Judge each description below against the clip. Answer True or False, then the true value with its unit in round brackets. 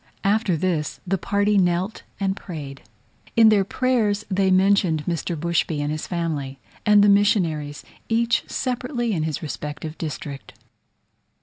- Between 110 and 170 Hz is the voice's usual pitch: False (185 Hz)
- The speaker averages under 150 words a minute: True (135 wpm)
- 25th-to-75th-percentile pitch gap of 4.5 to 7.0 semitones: True (4.9 semitones)